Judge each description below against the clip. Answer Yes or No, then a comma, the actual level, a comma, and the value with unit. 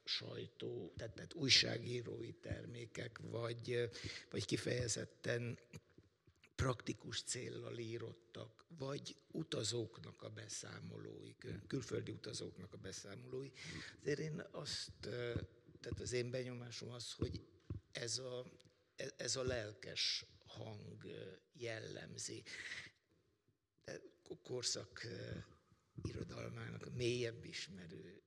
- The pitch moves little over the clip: Yes, narrow, 2.0 semitones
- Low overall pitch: Yes, low, 120 Hz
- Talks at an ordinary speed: No, slow, 90 wpm